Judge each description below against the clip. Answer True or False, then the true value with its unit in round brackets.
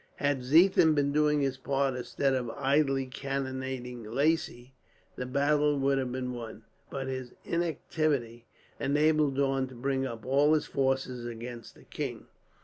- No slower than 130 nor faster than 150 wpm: True (145 wpm)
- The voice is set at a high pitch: False (135 Hz)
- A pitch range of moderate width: False (2.2 semitones)